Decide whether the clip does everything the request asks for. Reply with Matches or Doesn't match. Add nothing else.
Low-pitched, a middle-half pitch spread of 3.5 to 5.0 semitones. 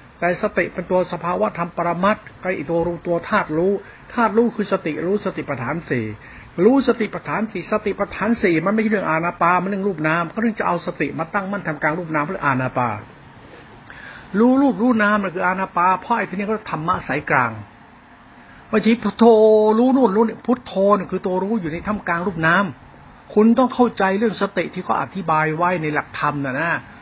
Doesn't match